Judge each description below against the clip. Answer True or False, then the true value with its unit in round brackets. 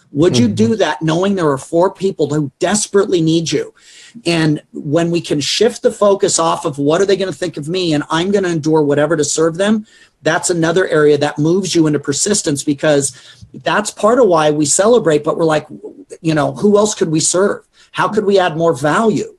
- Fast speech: True (215 wpm)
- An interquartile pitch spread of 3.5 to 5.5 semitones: True (4.4 semitones)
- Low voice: False (165 Hz)